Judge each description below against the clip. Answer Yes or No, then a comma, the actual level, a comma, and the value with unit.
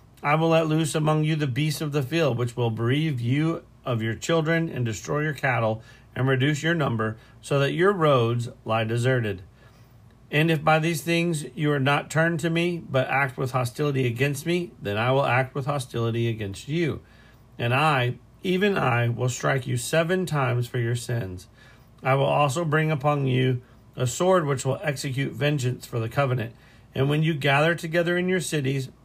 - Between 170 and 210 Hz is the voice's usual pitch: No, low, 135 Hz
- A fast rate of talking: No, average, 190 wpm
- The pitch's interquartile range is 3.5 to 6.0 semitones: Yes, average, 4.3 semitones